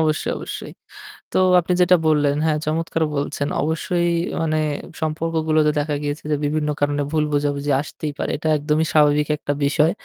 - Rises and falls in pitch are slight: Yes, narrow, 1.6 semitones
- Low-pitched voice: No, medium, 155 Hz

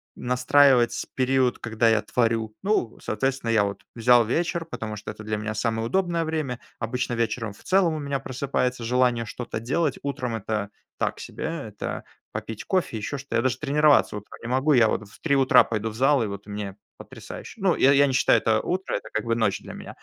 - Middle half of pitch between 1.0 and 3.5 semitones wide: No, average, 4.1 semitones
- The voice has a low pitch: Yes, low, 125 Hz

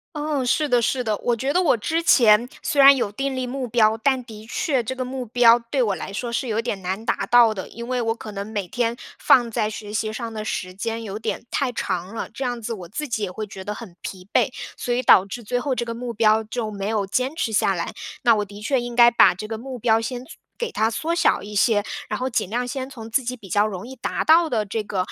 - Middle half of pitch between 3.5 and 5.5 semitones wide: No, average, 3.1 semitones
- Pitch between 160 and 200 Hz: No, high, 230 Hz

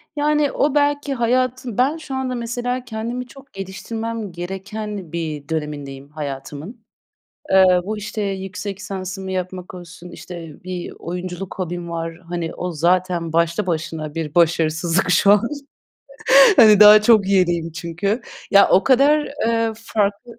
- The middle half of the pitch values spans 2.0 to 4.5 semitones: No, average, 5.1 semitones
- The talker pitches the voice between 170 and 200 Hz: Yes, high, 190 Hz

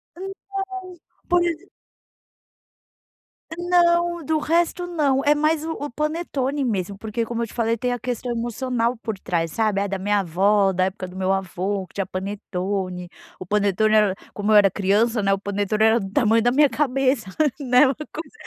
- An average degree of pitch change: No, wide, 6.7 semitones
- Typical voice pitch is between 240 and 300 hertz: No, high, 225 Hz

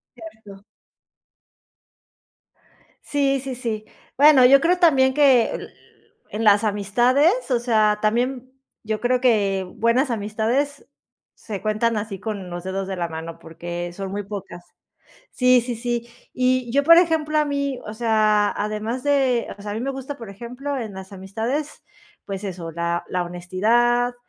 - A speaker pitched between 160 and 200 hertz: No, high, 230 Hz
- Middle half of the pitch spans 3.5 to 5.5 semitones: Yes, average, 4.5 semitones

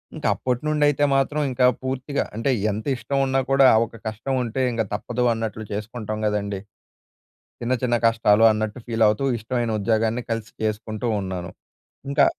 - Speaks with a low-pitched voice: Yes, low, 115 Hz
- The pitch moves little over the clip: No, average, 3.1 semitones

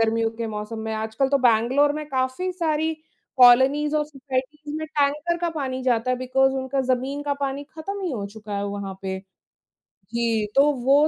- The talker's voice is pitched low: No, very high, 265 Hz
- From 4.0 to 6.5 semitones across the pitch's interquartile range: Yes, average, 4.4 semitones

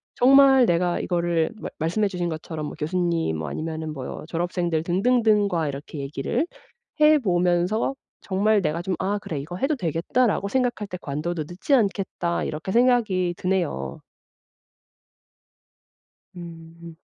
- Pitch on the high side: No, medium, 175 Hz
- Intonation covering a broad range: No, average, 4.2 semitones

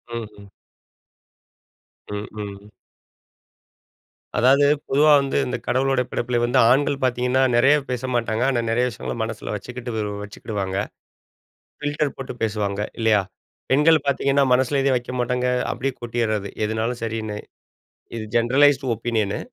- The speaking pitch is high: No, low, 120 Hz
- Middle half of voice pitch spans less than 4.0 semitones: Yes, average, 3.4 semitones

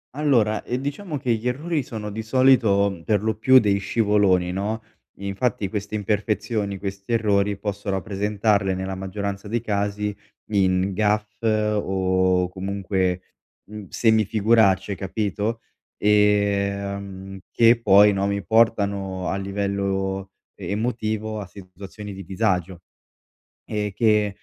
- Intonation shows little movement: Yes, narrow, 2.0 semitones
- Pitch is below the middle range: Yes, low, 100 Hz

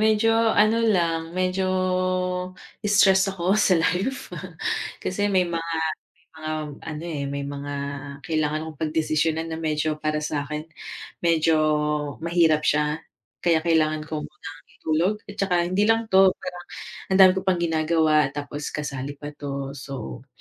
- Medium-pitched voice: Yes, medium, 160 Hz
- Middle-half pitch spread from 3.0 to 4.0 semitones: Yes, average, 3.6 semitones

